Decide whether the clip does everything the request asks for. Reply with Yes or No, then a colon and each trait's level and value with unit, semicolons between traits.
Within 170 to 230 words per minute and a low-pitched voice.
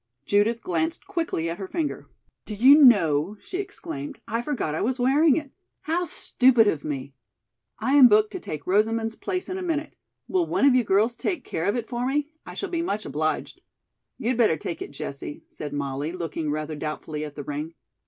No: average, 200 wpm; high, 220 Hz